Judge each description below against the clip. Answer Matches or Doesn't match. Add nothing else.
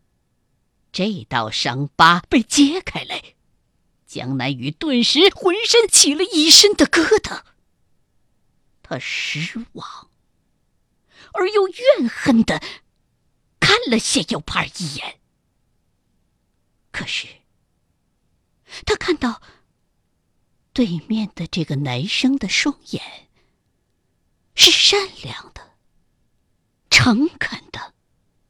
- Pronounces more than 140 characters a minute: Doesn't match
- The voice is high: Matches